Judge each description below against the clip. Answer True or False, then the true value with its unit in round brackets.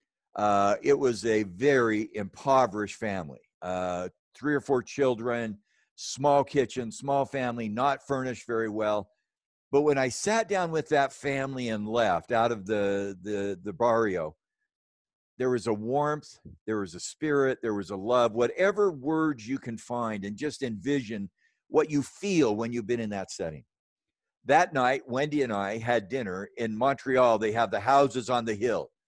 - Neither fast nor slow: True (165 wpm)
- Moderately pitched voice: False (120 Hz)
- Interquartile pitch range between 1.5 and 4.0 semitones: False (4.6 semitones)